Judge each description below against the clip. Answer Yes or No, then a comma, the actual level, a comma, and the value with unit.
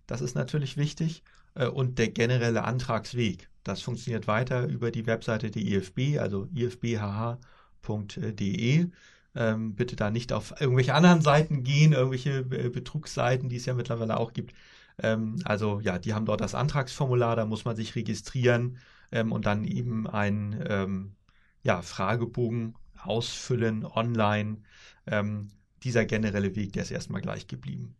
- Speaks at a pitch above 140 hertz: No, low, 115 Hz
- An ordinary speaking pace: Yes, average, 135 wpm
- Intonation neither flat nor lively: Yes, average, 3.1 semitones